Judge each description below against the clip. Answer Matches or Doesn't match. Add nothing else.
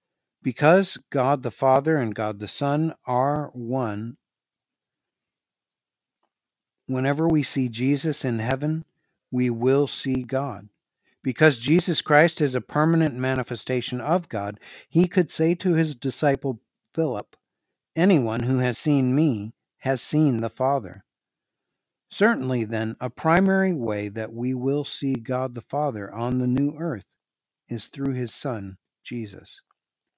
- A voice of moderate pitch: Doesn't match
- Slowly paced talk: Matches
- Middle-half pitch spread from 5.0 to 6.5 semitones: Doesn't match